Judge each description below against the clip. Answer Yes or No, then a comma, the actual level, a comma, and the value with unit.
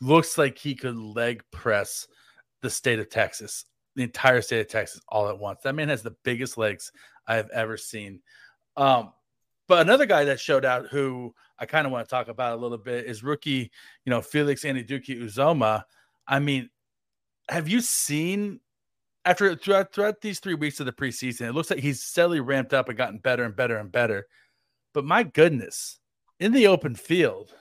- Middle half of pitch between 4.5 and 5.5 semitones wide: Yes, average, 5.0 semitones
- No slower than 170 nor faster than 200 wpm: Yes, average, 190 wpm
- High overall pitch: No, low, 135 Hz